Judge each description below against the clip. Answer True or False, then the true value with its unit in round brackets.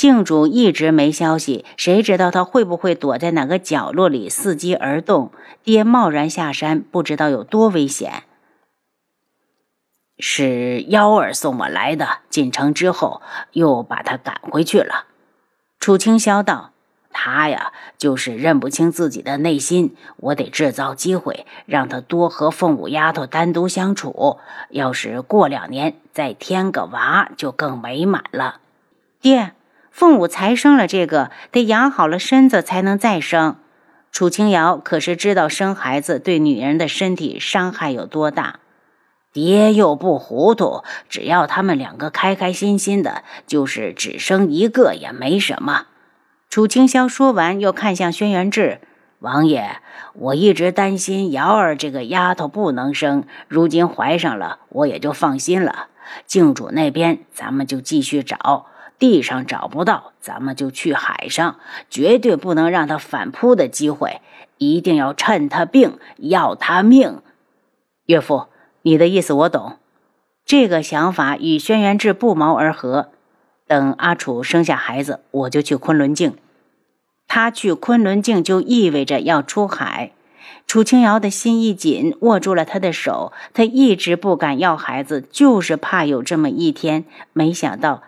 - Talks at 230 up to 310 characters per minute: False (220 characters per minute)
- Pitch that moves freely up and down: True (6.1 semitones)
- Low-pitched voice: False (180 Hz)